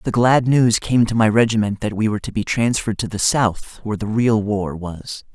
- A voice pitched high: No, low, 110 Hz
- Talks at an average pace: No, fast, 235 wpm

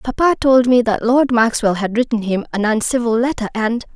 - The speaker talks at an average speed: Yes, average, 195 wpm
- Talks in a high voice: Yes, high, 235 Hz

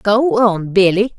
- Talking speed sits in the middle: Yes, average, 150 wpm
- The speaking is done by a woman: Yes, female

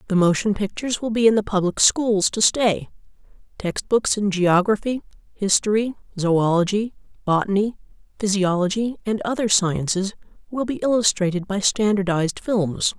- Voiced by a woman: Yes, female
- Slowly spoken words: Yes, slow, 130 wpm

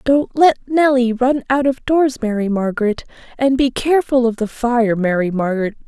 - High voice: Yes, high, 245 Hz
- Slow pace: No, average, 175 wpm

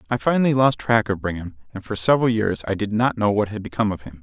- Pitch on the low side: Yes, low, 105 Hz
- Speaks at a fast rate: Yes, fast, 270 wpm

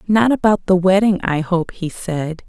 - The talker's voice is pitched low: No, medium, 185 Hz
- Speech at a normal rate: Yes, average, 195 wpm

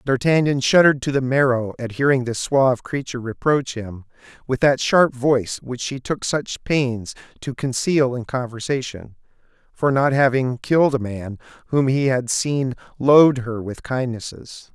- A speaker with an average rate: Yes, average, 160 wpm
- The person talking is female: No, male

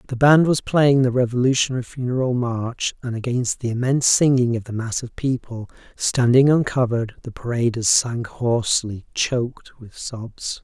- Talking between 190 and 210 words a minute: No, average, 150 wpm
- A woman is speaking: No, male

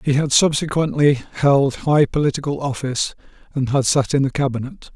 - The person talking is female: No, male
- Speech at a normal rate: Yes, average, 155 wpm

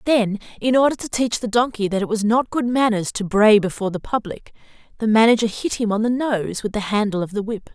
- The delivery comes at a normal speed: No, fast, 240 wpm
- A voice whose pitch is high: Yes, high, 220 Hz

